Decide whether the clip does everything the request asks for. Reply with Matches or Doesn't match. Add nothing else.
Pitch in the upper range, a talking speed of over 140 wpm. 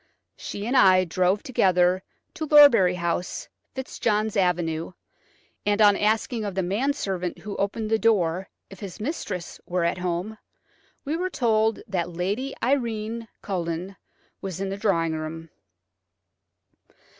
Doesn't match